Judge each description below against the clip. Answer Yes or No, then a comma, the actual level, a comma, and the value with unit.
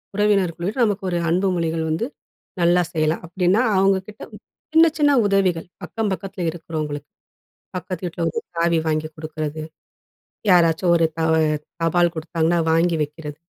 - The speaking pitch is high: No, medium, 170 Hz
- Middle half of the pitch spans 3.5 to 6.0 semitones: No, average, 2.9 semitones